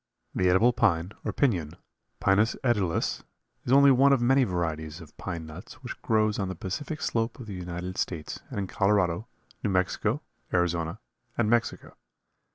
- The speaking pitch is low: Yes, very low, 95 Hz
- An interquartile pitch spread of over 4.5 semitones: Yes, average, 5.1 semitones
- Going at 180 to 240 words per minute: No, average, 165 wpm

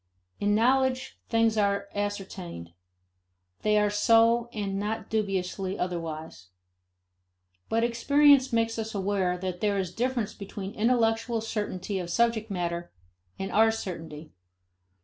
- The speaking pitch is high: Yes, high, 210 Hz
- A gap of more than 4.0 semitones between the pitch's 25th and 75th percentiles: No, average, 3.4 semitones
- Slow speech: Yes, slow, 120 wpm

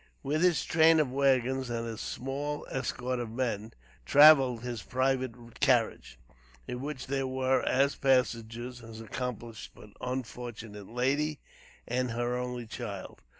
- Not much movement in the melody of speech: Yes, narrow, 2.3 semitones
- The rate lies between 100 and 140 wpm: Yes, slow, 135 wpm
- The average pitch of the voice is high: No, low, 125 Hz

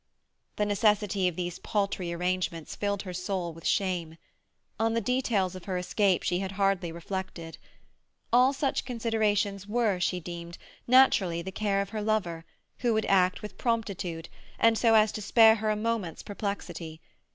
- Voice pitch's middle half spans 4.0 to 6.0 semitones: No, average, 3.4 semitones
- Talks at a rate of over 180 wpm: No, average, 165 wpm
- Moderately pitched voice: No, high, 200 Hz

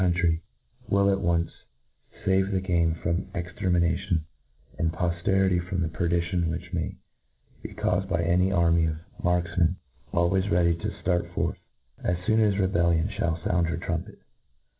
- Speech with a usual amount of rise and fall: No, narrow, 1.9 semitones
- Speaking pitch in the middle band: No, very low, 85 Hz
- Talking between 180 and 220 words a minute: No, average, 155 wpm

